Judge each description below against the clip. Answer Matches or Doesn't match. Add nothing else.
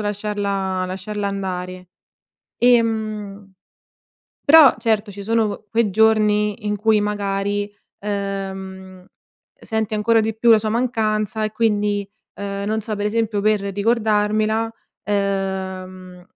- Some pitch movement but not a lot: Doesn't match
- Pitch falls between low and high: Doesn't match